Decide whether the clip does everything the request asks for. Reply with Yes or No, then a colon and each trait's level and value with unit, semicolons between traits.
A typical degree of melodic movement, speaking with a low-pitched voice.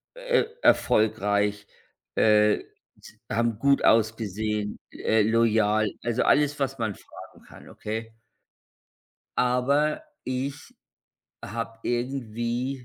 Yes: average, 3.3 semitones; low, 115 Hz